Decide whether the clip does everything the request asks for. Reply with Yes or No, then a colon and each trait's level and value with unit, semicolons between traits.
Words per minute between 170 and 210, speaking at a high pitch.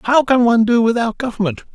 Yes: fast, 205 wpm; high, 230 Hz